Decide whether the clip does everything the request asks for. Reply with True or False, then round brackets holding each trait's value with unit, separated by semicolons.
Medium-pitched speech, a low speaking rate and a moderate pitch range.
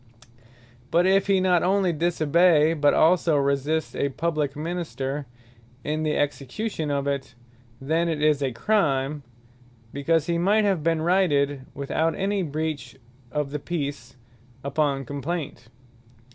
True (155 Hz; 130 wpm; 3.4 semitones)